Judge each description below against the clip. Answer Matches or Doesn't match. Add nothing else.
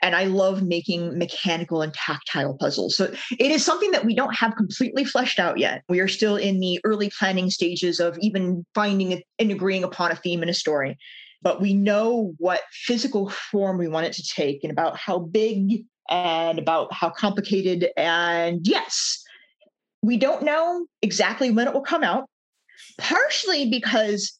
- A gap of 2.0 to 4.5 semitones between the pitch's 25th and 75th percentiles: Doesn't match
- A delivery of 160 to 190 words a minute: Matches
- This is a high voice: Matches